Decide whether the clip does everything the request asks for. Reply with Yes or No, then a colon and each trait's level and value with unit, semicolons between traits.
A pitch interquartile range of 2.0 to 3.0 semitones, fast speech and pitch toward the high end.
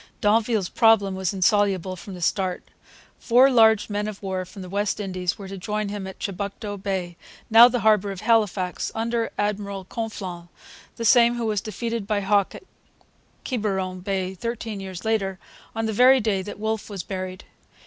No: average, 2.7 semitones; average, 175 wpm; high, 205 Hz